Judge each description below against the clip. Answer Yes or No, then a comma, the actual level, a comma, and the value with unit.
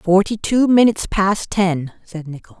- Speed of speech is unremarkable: Yes, average, 160 wpm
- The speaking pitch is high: Yes, high, 195 Hz